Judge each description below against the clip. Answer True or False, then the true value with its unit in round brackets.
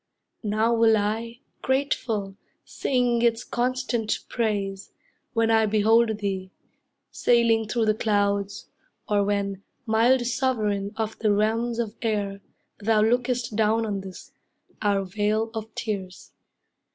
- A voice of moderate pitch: False (220 Hz)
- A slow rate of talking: True (120 wpm)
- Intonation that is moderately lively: False (2.3 semitones)